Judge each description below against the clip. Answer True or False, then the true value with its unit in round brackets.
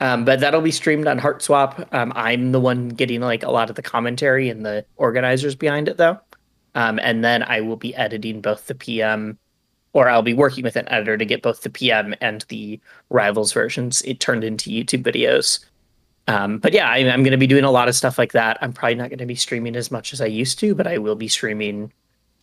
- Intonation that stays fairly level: False (3.2 semitones)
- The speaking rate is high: True (235 wpm)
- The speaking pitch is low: True (120 Hz)